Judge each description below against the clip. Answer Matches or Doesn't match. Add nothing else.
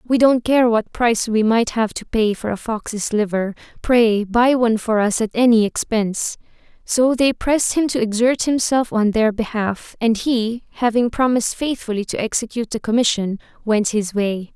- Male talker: Doesn't match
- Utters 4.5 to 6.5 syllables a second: Matches